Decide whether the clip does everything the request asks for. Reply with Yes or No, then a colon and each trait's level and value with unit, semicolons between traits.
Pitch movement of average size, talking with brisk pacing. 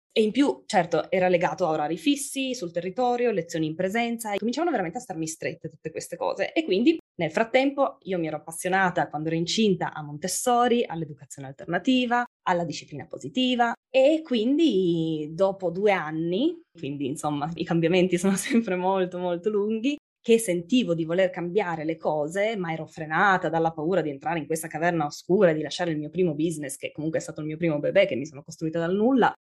No: wide, 6.2 semitones; fast, 190 wpm